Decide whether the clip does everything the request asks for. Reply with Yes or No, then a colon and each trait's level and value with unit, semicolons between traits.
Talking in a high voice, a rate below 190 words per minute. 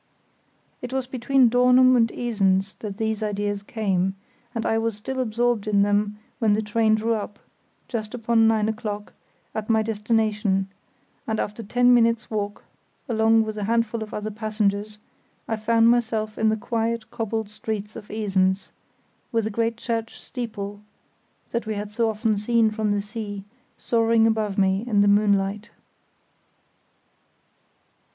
Yes: high, 220 Hz; average, 150 wpm